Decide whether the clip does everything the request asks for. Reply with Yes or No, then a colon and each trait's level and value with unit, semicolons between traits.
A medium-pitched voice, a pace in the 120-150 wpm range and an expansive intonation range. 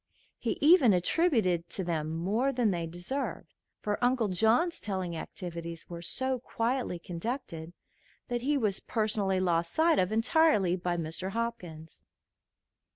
No: high, 195 Hz; slow, 135 wpm; wide, 6.2 semitones